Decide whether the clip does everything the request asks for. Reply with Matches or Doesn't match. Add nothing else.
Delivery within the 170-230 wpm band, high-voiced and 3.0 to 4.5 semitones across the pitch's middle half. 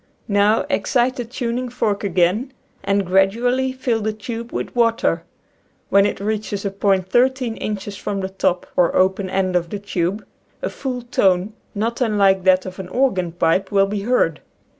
Matches